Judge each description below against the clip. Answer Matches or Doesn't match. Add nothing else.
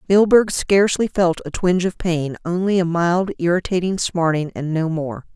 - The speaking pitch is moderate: Matches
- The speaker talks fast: Doesn't match